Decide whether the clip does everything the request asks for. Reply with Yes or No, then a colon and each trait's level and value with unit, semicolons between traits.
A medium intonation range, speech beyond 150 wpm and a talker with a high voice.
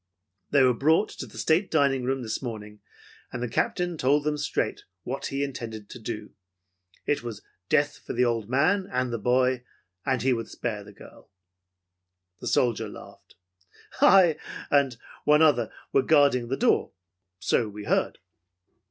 No: average, 3.6 semitones; average, 160 wpm; low, 130 Hz